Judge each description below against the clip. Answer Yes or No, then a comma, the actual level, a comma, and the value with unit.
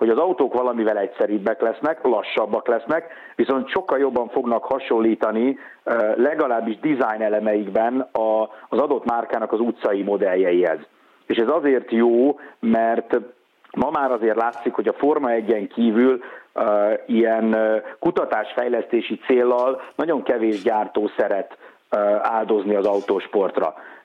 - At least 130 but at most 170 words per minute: No, average, 115 wpm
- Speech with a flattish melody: Yes, narrow, 2.2 semitones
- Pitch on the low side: Yes, low, 115 Hz